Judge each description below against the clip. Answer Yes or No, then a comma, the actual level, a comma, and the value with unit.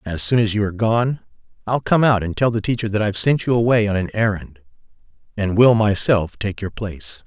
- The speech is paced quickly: Yes, fast, 225 wpm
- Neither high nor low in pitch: No, low, 105 Hz